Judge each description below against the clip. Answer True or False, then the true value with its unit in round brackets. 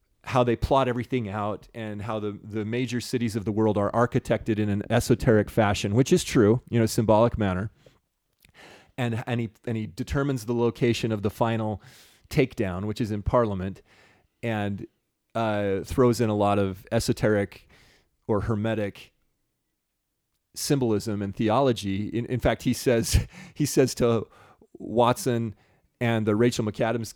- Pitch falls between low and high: False (115 Hz)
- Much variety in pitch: False (2.6 semitones)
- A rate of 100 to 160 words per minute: True (150 wpm)